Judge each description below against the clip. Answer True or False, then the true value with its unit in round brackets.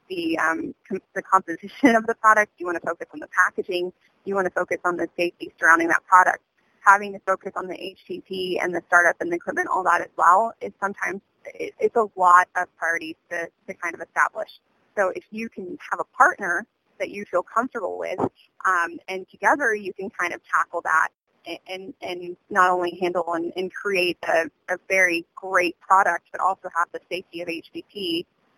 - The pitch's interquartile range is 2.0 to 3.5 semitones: True (2.6 semitones)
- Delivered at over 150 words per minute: True (200 wpm)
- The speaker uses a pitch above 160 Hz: True (185 Hz)